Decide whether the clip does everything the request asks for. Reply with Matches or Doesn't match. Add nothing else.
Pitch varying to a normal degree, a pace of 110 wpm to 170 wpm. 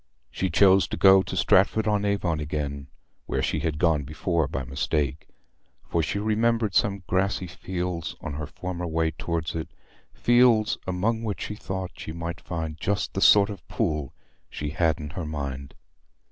Matches